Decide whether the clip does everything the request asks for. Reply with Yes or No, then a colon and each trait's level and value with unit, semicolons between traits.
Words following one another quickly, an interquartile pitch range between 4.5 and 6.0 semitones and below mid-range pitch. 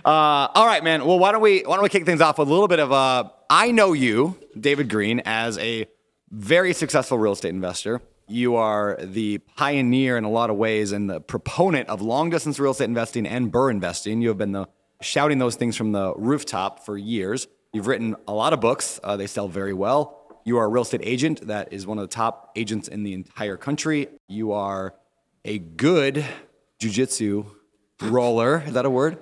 Yes: fast, 215 wpm; wide, 5.4 semitones; low, 115 Hz